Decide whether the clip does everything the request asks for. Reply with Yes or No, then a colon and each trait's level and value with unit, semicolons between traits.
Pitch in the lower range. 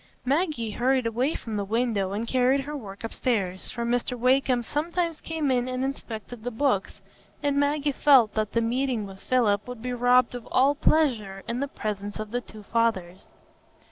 No: high, 245 Hz